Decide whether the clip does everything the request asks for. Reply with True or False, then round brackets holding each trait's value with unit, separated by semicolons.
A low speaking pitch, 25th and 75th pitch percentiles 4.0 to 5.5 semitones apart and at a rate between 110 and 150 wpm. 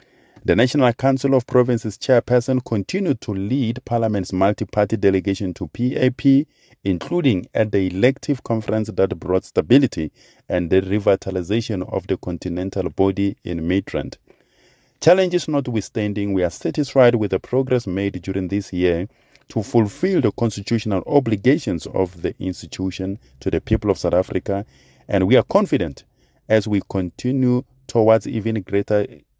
True (105 Hz; 4.7 semitones; 140 wpm)